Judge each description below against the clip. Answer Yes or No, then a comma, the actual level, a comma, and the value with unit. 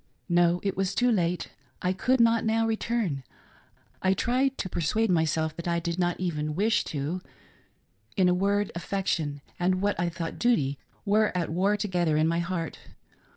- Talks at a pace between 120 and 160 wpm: No, average, 185 wpm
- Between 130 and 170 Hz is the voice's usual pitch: No, medium, 180 Hz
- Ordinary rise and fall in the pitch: Yes, average, 3.7 semitones